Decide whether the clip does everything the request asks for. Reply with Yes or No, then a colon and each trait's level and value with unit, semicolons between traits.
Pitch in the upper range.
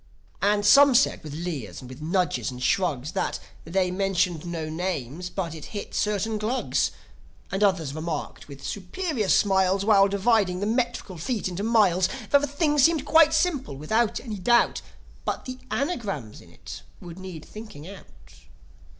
Yes: high, 195 Hz